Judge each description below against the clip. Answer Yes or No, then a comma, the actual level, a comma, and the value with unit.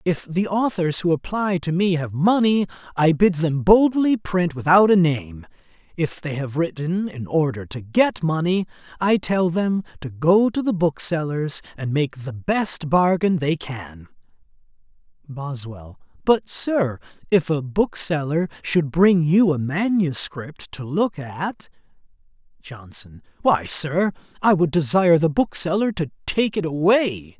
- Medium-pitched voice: Yes, medium, 165 Hz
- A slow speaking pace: No, average, 145 wpm